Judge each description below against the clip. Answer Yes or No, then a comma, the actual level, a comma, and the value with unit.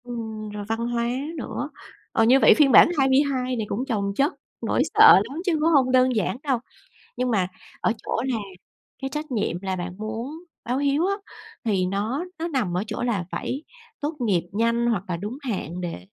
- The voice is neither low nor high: No, high, 235 Hz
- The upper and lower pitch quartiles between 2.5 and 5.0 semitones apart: Yes, average, 4.7 semitones